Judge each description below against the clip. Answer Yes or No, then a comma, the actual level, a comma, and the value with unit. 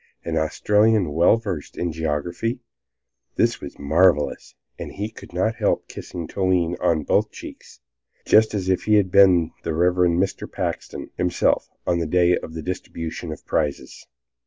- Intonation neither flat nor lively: Yes, average, 3.0 semitones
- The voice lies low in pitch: Yes, very low, 90 Hz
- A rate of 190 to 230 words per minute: No, average, 160 wpm